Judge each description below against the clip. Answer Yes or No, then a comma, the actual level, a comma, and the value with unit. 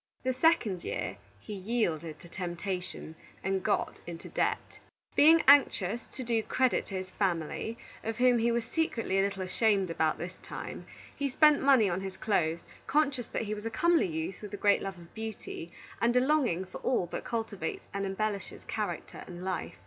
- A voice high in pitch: Yes, high, 205 Hz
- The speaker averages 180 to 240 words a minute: Yes, average, 185 wpm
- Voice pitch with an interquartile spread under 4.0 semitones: No, average, 4.7 semitones